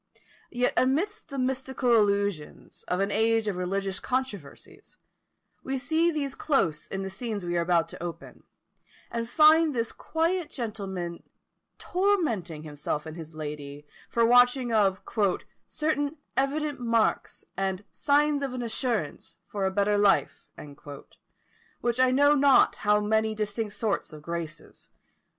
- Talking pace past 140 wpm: No, slow, 135 wpm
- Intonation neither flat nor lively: No, wide, 6.1 semitones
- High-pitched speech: Yes, high, 225 Hz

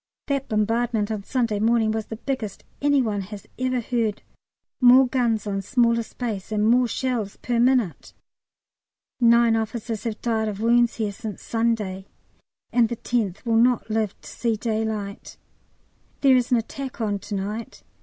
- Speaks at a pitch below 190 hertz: No, high, 225 Hz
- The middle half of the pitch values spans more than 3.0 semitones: No, narrow, 2.4 semitones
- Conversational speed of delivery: Yes, average, 160 wpm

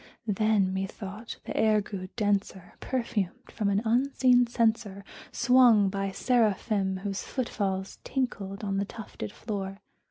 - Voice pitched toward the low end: No, high, 205 Hz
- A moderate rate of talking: No, slow, 130 wpm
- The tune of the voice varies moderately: Yes, average, 3.0 semitones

